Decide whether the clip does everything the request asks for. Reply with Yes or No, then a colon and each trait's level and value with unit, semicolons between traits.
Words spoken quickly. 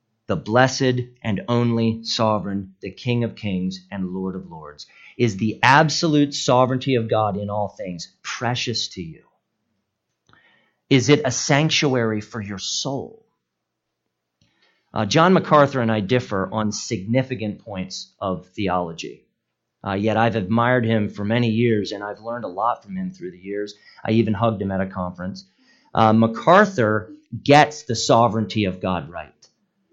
No: average, 150 wpm